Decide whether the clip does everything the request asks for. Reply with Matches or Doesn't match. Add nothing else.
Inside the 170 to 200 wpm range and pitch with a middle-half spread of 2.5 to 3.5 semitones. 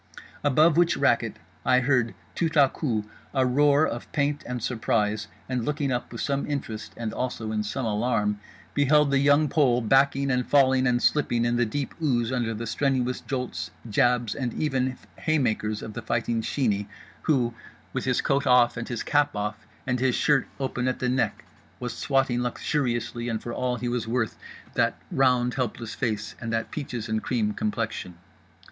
Matches